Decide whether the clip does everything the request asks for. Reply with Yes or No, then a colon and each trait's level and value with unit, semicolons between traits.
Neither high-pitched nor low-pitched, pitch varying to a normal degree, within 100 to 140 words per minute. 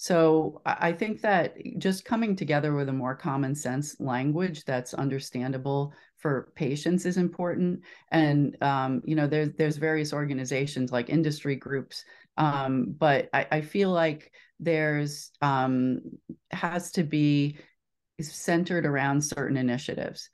Yes: medium, 150 Hz; average, 3.6 semitones; slow, 135 wpm